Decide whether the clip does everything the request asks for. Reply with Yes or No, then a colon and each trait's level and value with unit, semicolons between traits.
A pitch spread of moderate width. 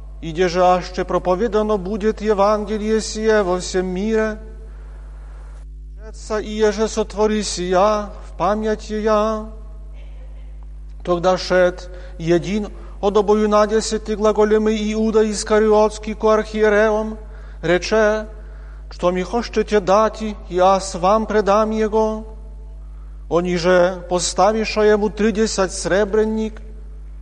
Yes: average, 3.3 semitones